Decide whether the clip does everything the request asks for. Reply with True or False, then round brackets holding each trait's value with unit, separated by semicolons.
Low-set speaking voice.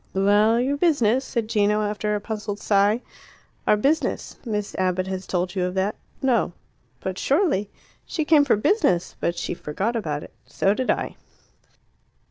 False (210 Hz)